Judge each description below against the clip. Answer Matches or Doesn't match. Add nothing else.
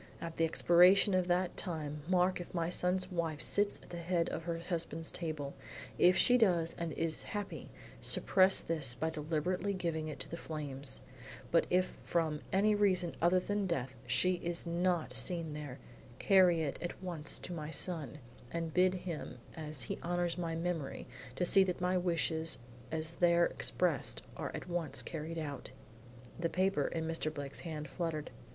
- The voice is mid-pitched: Matches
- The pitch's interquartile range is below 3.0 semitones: Matches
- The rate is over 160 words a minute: Matches